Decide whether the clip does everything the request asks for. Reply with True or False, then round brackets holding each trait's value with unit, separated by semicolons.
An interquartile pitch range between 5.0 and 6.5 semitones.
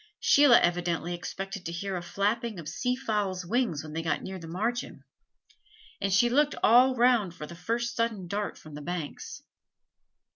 True (5.4 semitones)